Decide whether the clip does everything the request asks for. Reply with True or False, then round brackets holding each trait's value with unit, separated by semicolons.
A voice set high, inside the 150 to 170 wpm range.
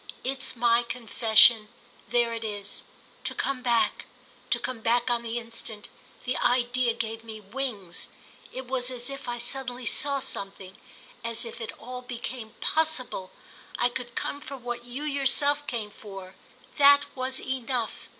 False (240 Hz; 140 wpm)